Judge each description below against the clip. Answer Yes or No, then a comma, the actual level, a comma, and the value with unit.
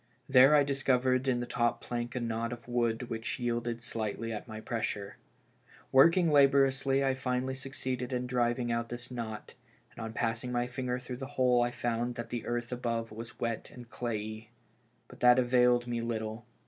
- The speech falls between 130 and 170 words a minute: No, average, 185 wpm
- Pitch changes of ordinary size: No, narrow, 1.5 semitones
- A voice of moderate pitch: No, low, 120 Hz